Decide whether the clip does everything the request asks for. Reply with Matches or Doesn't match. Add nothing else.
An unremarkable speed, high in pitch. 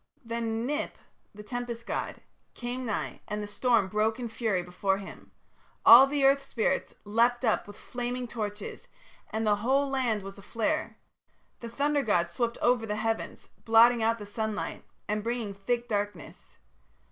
Matches